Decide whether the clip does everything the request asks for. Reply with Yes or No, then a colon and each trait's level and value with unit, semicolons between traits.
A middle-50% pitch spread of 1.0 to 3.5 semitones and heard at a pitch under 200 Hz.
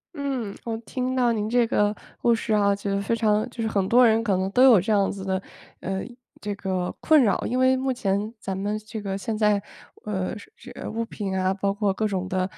No: average, 2.8 semitones; high, 210 Hz